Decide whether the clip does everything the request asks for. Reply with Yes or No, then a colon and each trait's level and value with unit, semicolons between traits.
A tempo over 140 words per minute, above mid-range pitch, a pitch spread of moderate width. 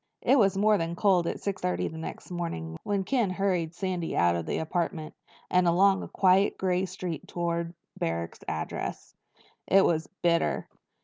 No: average, 165 wpm; medium, 175 Hz; average, 3.0 semitones